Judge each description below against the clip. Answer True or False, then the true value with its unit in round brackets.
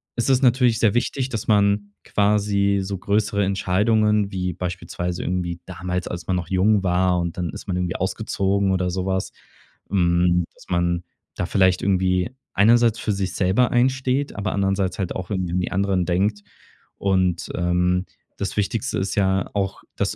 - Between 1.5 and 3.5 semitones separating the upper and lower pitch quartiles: True (2.4 semitones)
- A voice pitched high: False (95 Hz)